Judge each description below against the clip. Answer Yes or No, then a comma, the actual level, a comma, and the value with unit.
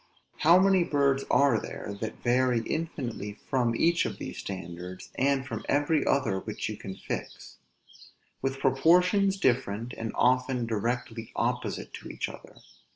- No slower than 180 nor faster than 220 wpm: No, average, 145 wpm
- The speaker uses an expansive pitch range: No, average, 4.1 semitones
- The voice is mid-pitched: No, low, 130 Hz